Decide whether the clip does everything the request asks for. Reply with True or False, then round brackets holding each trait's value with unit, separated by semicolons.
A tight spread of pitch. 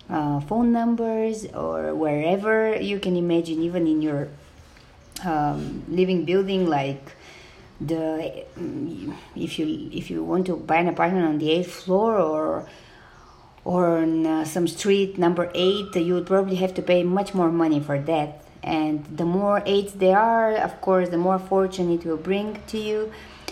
False (3.6 semitones)